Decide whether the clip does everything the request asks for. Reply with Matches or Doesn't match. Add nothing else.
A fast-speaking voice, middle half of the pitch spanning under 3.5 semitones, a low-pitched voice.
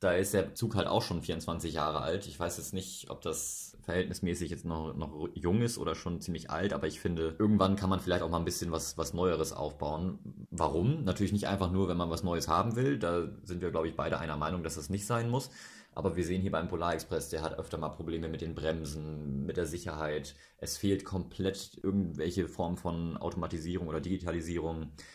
Matches